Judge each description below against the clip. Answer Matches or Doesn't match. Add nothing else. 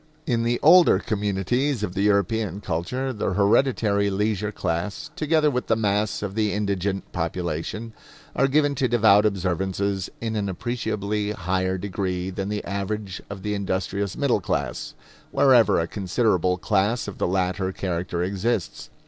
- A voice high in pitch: Doesn't match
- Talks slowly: Doesn't match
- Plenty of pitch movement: Doesn't match